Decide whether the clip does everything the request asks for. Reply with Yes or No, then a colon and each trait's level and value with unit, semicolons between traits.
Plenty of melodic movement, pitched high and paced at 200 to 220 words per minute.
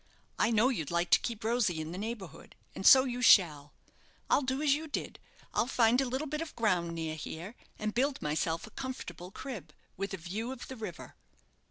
Yes: wide, 7.1 semitones; high, 220 Hz; fast, 205 wpm